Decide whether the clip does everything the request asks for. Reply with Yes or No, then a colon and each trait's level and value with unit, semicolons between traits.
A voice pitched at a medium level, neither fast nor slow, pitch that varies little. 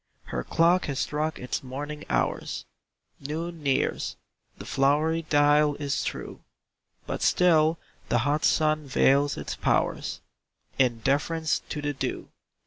No: medium, 150 Hz; slow, 130 wpm; narrow, 2.3 semitones